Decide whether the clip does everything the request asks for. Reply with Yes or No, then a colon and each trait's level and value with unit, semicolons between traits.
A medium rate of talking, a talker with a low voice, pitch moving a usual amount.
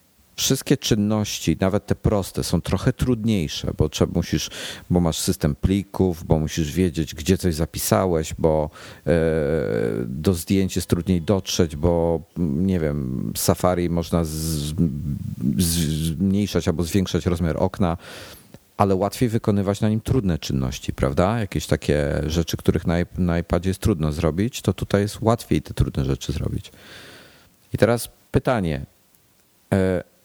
Yes: average, 140 wpm; very low, 90 Hz; average, 3.9 semitones